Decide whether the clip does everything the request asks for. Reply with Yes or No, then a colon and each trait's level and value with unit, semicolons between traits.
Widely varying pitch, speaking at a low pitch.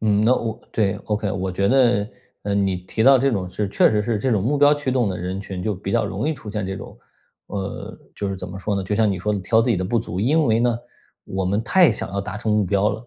No: average, 3.1 semitones; low, 105 Hz